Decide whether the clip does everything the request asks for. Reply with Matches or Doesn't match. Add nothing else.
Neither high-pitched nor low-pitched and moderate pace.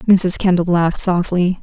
Matches